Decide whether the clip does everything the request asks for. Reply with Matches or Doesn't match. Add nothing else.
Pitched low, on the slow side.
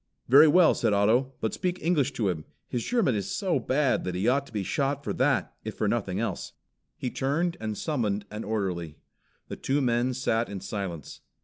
Doesn't match